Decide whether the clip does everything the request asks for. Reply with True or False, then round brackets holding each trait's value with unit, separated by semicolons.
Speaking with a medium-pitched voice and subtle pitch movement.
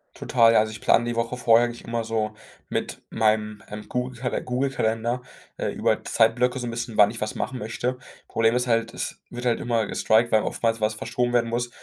False (115 Hz; 1.6 semitones)